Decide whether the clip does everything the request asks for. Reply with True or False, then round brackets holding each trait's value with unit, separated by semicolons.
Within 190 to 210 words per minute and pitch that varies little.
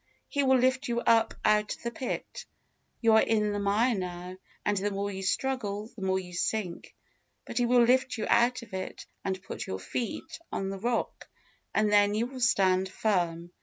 False (200 wpm; 3.8 semitones)